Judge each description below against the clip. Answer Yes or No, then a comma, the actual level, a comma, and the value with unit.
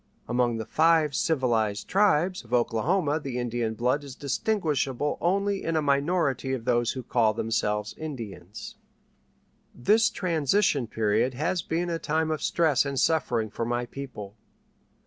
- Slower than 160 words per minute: Yes, average, 145 wpm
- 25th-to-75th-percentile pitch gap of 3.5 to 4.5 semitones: No, wide, 5.4 semitones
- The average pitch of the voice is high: No, low, 135 Hz